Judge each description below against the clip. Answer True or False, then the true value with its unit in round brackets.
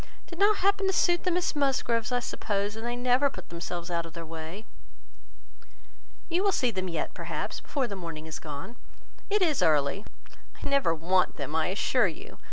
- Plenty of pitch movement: True (9.0 semitones)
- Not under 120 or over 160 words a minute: False (195 wpm)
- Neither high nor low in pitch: False (210 Hz)